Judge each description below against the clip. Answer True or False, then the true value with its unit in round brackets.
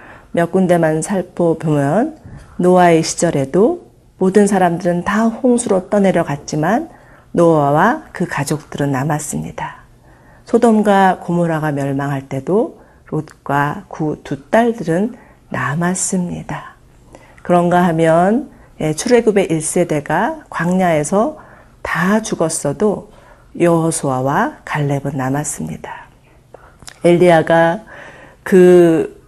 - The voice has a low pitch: False (170 Hz)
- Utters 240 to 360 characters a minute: False (220 characters per minute)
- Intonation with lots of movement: False (4.2 semitones)